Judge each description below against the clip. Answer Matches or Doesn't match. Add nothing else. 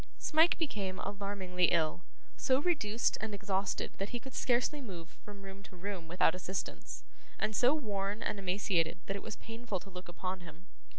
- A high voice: Matches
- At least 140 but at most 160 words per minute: Doesn't match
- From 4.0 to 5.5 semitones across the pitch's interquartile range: Doesn't match